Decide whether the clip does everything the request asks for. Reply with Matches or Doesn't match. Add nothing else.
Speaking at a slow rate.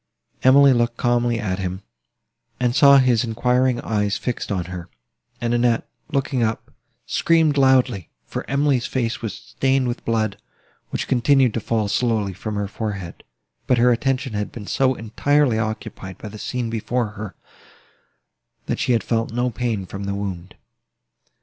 Doesn't match